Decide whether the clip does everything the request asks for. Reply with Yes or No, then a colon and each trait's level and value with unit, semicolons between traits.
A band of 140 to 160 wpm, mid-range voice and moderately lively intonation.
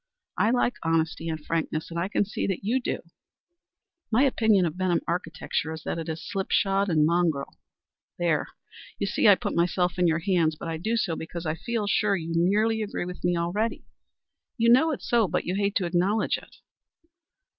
No: average, 200 wpm; medium, 180 Hz; average, 4.1 semitones